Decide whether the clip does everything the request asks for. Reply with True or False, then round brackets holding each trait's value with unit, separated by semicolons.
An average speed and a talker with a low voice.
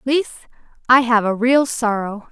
False (155 wpm; 235 Hz)